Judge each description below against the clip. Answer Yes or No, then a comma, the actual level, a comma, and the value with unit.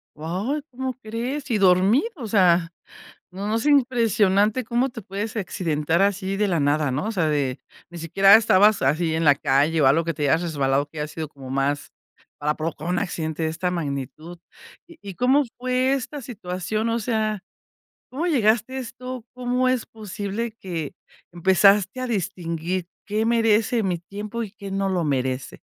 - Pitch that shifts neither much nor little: No, wide, 5.9 semitones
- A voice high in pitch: Yes, high, 195 Hz